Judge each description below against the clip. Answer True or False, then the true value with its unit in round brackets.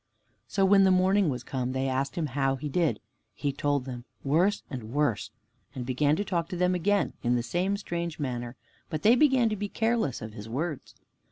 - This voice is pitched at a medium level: True (150 Hz)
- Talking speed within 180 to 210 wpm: True (205 wpm)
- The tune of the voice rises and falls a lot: True (6.5 semitones)